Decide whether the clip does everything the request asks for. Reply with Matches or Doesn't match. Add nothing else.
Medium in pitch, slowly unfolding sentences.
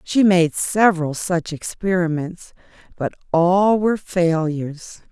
Matches